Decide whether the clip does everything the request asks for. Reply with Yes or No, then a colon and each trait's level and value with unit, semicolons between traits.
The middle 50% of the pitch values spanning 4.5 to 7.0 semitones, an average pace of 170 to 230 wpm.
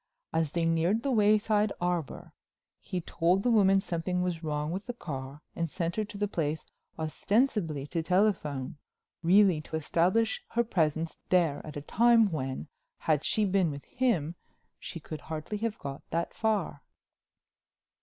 No: average, 4.9 semitones; average, 155 wpm